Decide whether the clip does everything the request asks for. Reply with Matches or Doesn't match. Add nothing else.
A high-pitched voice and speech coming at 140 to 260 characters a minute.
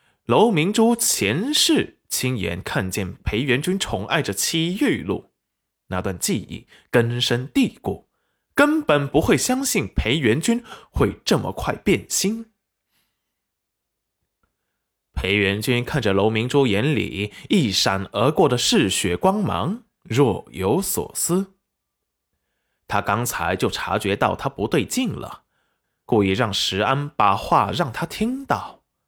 Doesn't match